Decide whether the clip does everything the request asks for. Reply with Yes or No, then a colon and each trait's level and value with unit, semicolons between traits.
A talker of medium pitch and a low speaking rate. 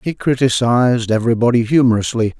No: low, 120 Hz; slow, 100 wpm